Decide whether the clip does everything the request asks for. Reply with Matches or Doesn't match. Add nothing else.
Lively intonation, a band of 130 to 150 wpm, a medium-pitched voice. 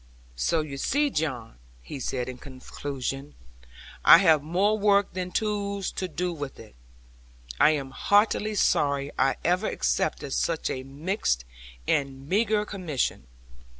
Matches